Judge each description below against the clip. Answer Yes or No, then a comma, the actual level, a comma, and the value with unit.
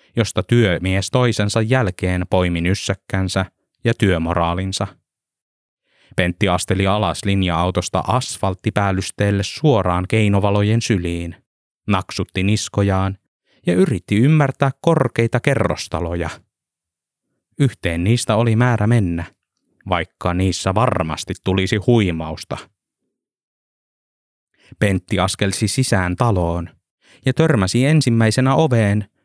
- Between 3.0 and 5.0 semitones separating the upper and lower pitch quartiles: Yes, average, 4.2 semitones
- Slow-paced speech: Yes, slow, 85 wpm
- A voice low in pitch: Yes, low, 100 Hz